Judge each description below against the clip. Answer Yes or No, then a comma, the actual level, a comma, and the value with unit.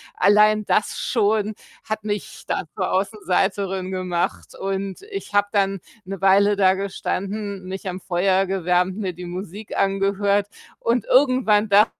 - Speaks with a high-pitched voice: Yes, high, 195 Hz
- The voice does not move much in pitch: Yes, narrow, 1.8 semitones